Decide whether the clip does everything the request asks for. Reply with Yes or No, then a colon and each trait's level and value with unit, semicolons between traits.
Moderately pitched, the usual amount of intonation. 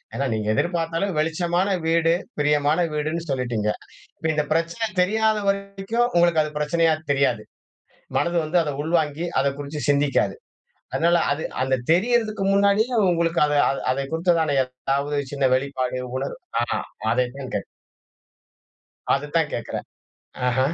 Yes: medium, 160 Hz; average, 3.8 semitones